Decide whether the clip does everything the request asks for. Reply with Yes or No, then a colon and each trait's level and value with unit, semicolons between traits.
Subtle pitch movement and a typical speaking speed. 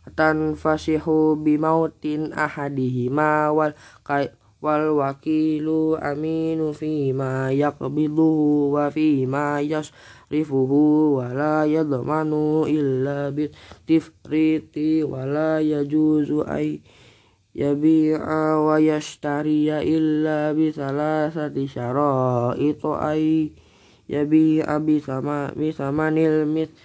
No: narrow, 1.5 semitones; slow, 65 wpm